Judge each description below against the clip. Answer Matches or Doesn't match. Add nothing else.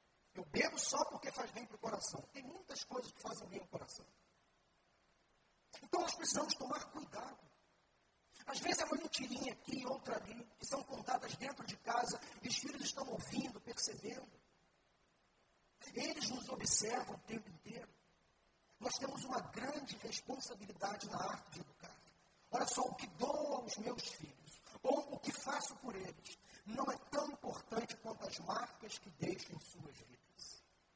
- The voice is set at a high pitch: Matches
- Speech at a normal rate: Matches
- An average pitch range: Matches